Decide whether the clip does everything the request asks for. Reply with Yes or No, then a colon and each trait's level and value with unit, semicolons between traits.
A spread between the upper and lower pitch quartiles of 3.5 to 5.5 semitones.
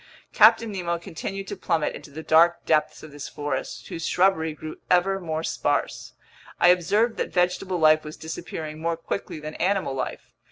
No: average, 3.0 semitones